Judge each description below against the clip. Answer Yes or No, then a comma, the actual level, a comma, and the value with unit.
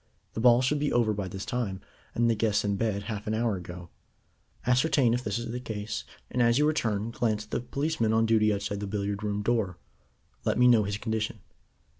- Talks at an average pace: No, fast, 215 wpm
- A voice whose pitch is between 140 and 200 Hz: No, low, 110 Hz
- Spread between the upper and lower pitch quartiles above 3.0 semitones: No, average, 2.7 semitones